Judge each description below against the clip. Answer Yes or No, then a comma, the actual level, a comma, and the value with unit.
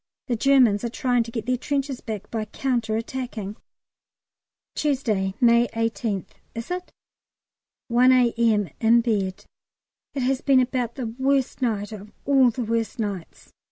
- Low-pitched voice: No, high, 235 Hz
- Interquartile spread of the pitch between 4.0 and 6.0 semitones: No, average, 3.0 semitones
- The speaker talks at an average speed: Yes, average, 145 wpm